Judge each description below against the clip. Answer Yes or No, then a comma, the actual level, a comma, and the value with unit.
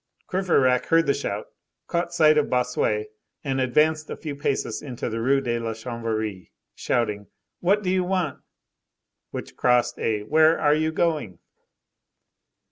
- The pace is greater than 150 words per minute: No, average, 145 wpm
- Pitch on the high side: No, low, 135 Hz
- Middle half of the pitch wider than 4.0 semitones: Yes, average, 5.2 semitones